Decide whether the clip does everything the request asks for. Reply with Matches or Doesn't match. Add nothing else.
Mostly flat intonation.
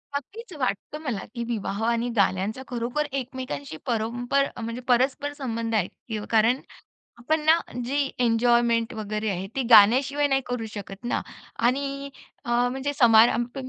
Doesn't match